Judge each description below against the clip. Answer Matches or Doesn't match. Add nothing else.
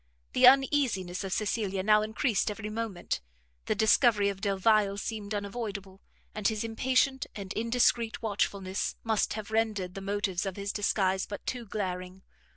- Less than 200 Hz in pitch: Doesn't match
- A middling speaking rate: Matches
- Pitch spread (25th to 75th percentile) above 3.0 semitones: Doesn't match